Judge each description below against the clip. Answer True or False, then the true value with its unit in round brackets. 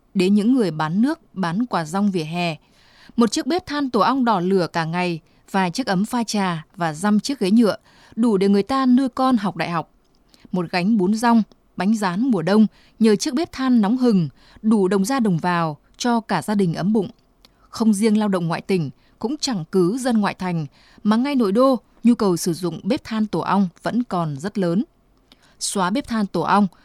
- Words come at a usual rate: True (215 wpm)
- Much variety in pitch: False (4.9 semitones)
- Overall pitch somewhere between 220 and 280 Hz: False (205 Hz)